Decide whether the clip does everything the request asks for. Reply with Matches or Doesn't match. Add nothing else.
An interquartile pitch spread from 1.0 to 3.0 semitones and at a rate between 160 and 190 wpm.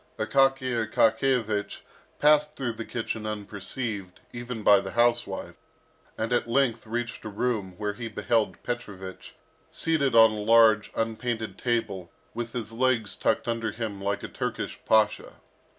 Doesn't match